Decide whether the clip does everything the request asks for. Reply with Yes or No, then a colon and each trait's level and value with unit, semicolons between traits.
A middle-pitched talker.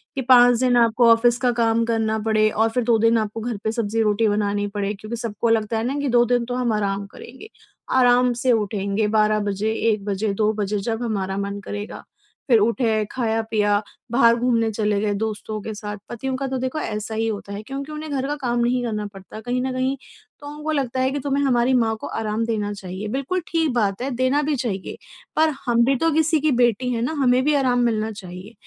No: high, 230 Hz